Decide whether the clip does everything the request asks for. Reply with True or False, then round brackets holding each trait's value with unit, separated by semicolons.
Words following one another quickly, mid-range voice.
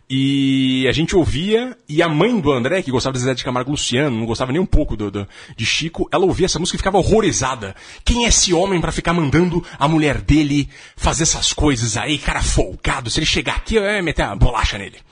True (230 wpm; 150 Hz)